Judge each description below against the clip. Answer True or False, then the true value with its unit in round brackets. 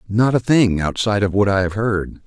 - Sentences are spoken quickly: True (240 wpm)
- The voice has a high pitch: False (105 Hz)